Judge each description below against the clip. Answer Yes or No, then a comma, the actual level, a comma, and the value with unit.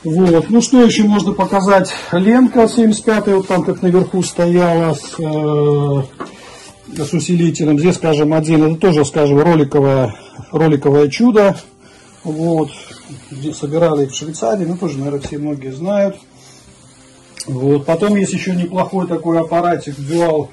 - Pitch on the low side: No, medium, 165 Hz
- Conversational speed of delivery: Yes, average, 130 wpm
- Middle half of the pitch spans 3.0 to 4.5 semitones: Yes, average, 4.1 semitones